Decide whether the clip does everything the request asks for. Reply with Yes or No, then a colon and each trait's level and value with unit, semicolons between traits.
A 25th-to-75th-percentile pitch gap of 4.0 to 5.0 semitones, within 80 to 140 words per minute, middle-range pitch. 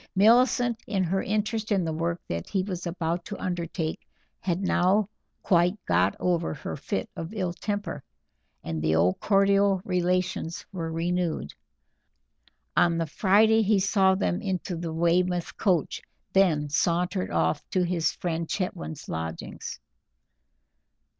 No: average, 3.0 semitones; slow, 135 wpm; medium, 180 Hz